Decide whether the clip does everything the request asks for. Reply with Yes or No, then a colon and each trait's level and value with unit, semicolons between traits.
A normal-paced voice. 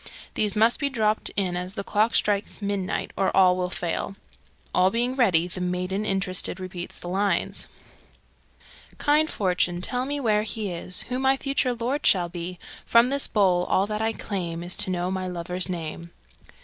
Yes: average, 175 wpm